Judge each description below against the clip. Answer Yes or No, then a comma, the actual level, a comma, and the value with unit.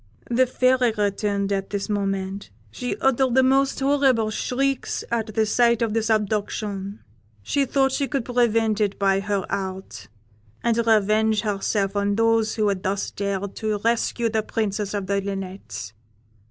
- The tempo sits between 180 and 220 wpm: No, average, 155 wpm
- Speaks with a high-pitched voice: Yes, high, 215 Hz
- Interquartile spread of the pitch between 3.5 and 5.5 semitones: No, average, 2.9 semitones